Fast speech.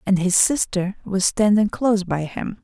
No: average, 180 wpm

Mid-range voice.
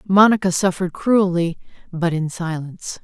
Yes: medium, 180 Hz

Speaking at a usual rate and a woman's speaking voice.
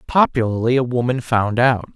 No: average, 155 wpm; male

